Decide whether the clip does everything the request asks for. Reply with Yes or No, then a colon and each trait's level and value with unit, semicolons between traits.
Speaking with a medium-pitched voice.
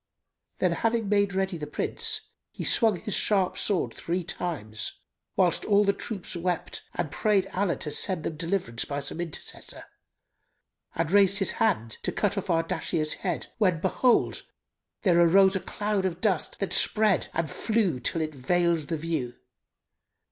Yes: medium, 180 Hz